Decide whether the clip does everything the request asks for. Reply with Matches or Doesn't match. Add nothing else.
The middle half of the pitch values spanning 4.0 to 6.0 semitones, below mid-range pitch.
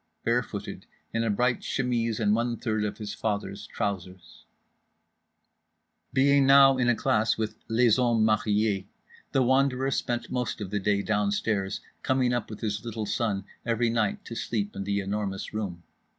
Doesn't match